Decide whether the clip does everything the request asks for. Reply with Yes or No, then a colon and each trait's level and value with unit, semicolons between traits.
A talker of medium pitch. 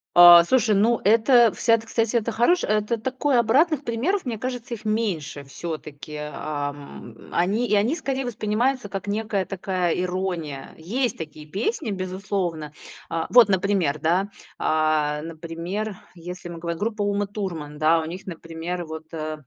No: high, 195 Hz